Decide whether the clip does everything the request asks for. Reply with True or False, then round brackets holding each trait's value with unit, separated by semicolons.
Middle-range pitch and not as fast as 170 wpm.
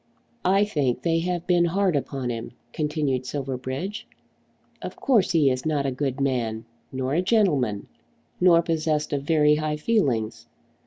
True (150 Hz; 150 wpm)